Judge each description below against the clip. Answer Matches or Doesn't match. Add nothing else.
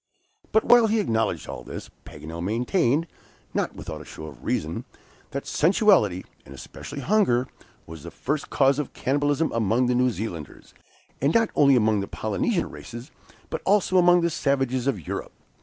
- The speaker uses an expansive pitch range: Matches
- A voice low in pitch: Matches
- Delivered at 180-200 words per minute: Doesn't match